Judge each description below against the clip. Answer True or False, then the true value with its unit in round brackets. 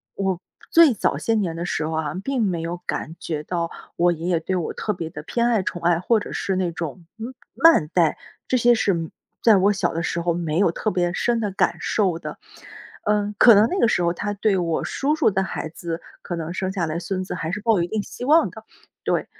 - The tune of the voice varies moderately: True (4.2 semitones)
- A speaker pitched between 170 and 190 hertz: True (185 Hz)